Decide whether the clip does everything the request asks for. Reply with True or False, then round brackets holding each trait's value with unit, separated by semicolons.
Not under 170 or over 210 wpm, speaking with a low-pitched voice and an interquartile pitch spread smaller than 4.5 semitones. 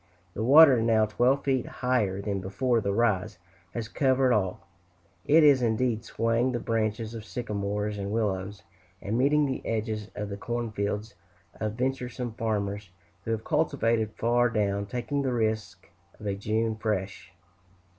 False (155 wpm; 110 Hz; 3.1 semitones)